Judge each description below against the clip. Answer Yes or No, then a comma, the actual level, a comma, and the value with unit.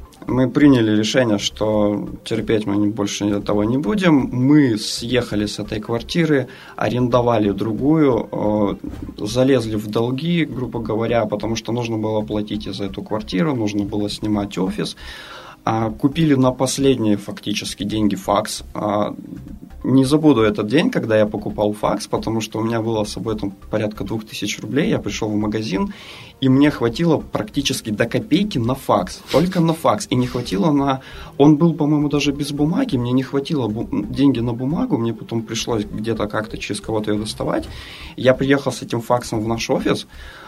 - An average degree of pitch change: Yes, average, 4.3 semitones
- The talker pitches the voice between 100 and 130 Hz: Yes, low, 115 Hz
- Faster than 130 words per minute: Yes, fast, 160 wpm